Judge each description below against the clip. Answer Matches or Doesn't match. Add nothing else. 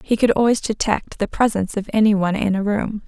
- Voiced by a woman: Matches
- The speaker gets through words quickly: Matches